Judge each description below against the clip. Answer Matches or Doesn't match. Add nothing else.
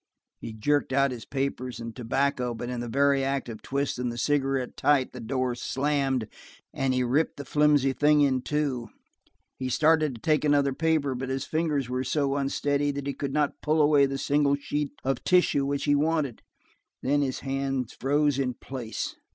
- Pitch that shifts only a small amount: Matches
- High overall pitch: Doesn't match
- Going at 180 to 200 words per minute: Matches